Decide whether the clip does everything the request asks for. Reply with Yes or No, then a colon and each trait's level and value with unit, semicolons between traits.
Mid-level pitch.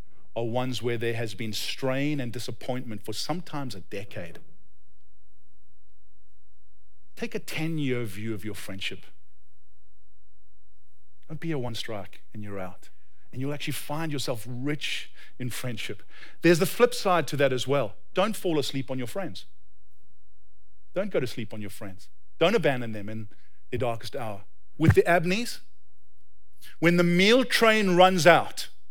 No: low, 110 Hz